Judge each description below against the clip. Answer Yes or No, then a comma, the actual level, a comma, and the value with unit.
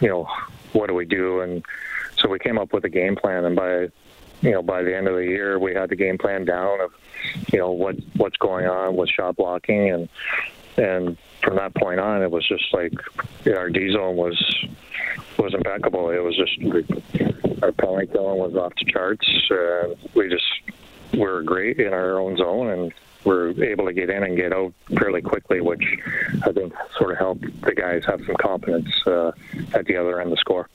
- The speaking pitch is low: Yes, very low, 90 Hz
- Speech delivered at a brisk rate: Yes, fast, 210 wpm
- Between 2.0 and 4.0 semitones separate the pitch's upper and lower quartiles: No, narrow, 1.2 semitones